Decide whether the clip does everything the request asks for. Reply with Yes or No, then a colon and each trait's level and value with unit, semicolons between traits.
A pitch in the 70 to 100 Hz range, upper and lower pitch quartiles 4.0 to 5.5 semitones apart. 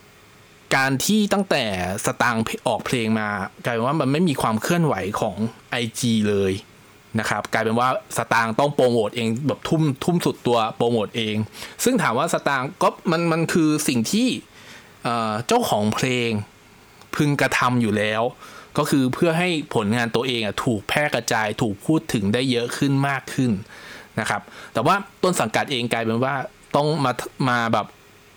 No: low, 125 Hz; average, 5.2 semitones